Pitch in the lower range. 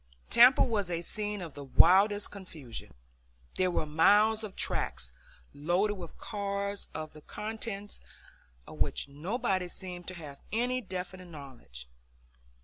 No: medium, 185 Hz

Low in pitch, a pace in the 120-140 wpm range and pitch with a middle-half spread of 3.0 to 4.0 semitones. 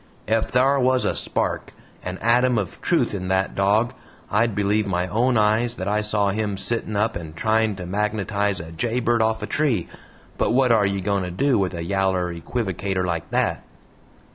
No: low, 105 Hz; average, 190 wpm; average, 3.3 semitones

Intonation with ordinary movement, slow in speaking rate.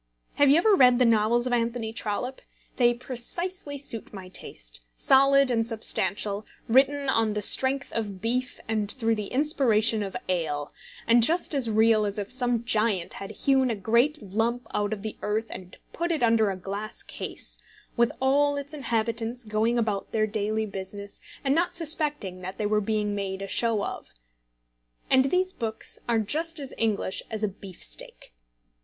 No: average, 4.1 semitones; average, 175 wpm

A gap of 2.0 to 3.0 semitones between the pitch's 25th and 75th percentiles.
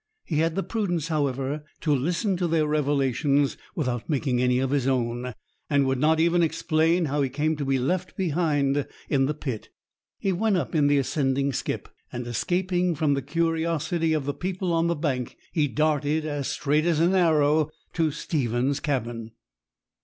No: average, 3.4 semitones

